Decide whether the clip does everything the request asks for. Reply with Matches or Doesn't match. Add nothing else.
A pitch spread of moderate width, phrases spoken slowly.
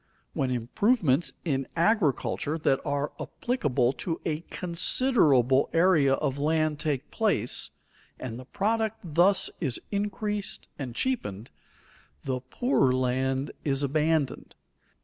Doesn't match